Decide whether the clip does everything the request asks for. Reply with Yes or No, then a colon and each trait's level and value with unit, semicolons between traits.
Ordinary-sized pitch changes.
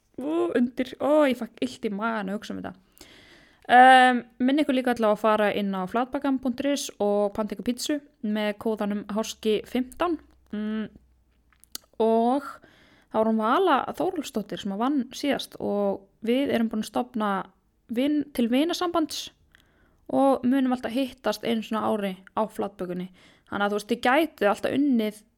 Yes: average, 4.2 semitones